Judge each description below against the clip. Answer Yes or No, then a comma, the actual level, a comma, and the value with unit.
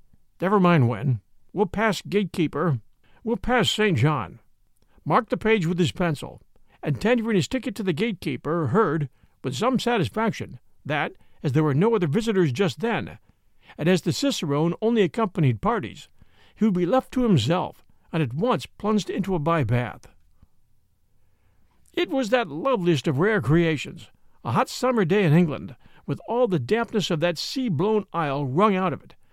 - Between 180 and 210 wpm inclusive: No, average, 165 wpm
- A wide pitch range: Yes, wide, 6.7 semitones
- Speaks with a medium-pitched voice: Yes, medium, 180 Hz